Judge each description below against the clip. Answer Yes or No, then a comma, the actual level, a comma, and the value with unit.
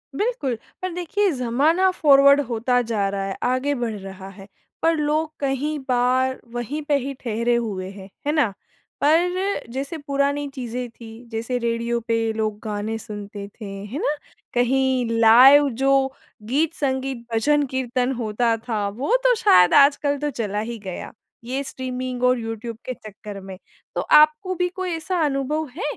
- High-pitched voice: Yes, very high, 255 Hz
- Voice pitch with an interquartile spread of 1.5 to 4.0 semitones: No, average, 4.4 semitones